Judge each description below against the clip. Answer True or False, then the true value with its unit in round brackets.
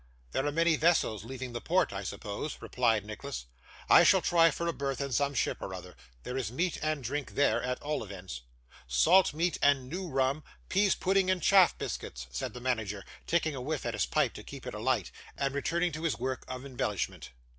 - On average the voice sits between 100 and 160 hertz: True (140 Hz)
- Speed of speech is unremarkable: False (210 wpm)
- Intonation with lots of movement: True (5.7 semitones)